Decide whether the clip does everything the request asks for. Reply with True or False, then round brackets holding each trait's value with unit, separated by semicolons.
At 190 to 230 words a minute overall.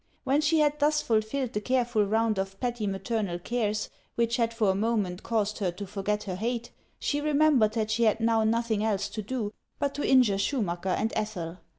True (200 wpm)